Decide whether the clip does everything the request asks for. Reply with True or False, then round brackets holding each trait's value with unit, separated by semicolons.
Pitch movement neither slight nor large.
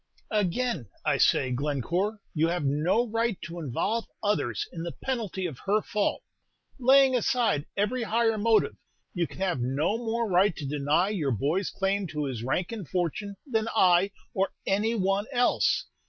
False (5.9 semitones)